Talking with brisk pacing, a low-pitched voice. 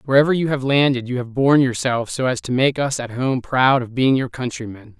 Yes: fast, 240 wpm; low, 130 Hz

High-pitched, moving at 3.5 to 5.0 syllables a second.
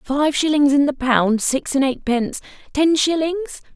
Yes: very high, 285 Hz; 4.3 syllables/s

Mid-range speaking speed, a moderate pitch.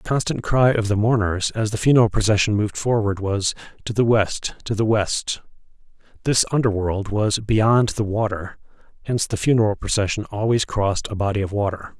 No: average, 180 wpm; low, 105 Hz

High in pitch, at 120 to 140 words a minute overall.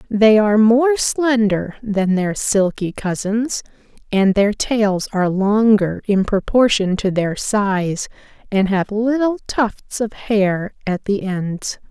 Yes: high, 210 Hz; slow, 135 wpm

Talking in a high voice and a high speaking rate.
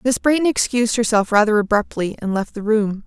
No: high, 220 Hz; average, 195 wpm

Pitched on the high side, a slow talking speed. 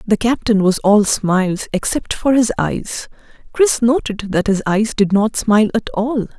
No: high, 215 Hz; average, 180 wpm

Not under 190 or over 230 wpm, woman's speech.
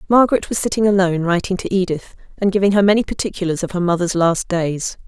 Yes: average, 200 wpm; female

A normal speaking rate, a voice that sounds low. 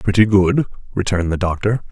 Yes: average, 155 wpm; low, 100 Hz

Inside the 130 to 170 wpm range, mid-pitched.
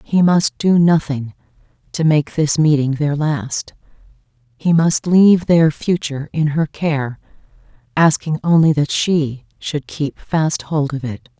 Yes: average, 145 wpm; medium, 150 Hz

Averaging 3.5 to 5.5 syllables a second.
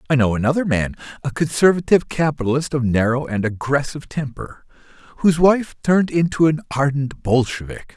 No: 5.8 syllables/s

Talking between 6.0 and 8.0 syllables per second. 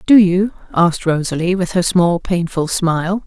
No: 4.8 syllables/s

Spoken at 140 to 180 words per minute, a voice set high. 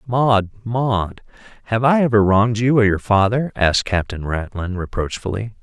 No: average, 150 wpm; low, 110 Hz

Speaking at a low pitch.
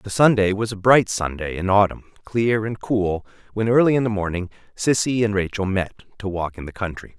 Yes: low, 105 Hz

